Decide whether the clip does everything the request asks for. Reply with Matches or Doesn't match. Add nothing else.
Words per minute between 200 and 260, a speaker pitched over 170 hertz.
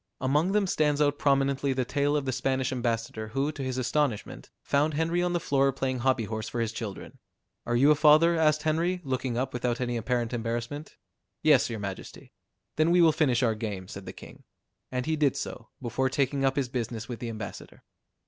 Doesn't match